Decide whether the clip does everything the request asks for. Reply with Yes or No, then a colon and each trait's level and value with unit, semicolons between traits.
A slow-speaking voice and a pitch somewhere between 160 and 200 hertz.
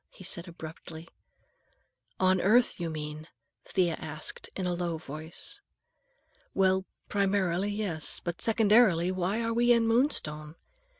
Yes: slow, 125 wpm; medium, 185 Hz